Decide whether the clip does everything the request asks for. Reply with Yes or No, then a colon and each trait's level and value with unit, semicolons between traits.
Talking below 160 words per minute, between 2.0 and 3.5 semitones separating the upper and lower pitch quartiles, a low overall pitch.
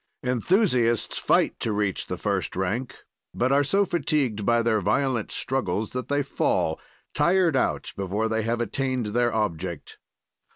No: average, 150 wpm; average, 4.3 semitones; low, 120 Hz